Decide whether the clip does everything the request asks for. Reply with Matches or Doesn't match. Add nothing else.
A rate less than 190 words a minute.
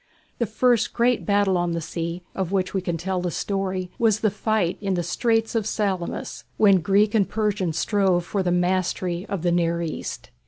Doesn't match